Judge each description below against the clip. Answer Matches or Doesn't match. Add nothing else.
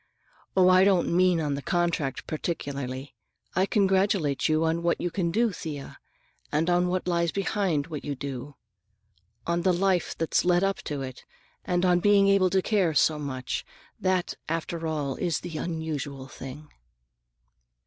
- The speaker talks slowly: Doesn't match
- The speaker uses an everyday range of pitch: Matches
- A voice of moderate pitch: Matches